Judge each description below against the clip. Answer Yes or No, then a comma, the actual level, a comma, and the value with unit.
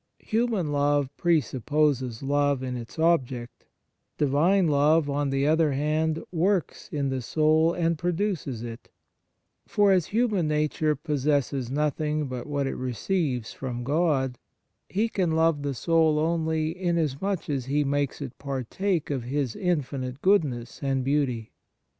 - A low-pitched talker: No, medium, 145 Hz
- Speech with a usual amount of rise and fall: Yes, average, 3.5 semitones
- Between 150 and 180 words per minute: No, slow, 135 wpm